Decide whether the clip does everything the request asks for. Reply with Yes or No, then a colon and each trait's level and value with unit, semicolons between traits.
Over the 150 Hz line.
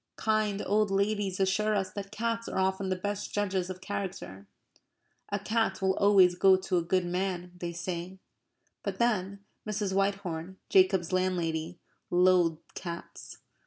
Yes: high, 190 Hz